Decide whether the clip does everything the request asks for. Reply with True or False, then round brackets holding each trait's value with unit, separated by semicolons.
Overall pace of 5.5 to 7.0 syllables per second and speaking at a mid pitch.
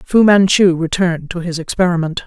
True (5.6 syllables/s; 175 Hz)